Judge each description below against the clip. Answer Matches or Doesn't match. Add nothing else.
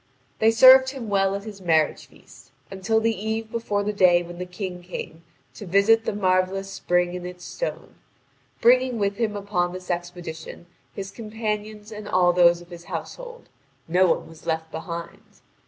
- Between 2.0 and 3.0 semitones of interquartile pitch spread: Doesn't match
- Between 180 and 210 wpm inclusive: Doesn't match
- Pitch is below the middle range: Doesn't match